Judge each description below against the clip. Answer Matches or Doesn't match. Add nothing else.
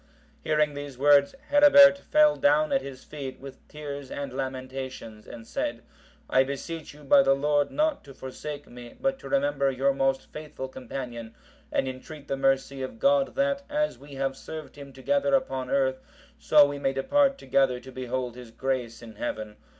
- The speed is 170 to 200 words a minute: Matches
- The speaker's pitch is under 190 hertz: Matches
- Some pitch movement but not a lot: Matches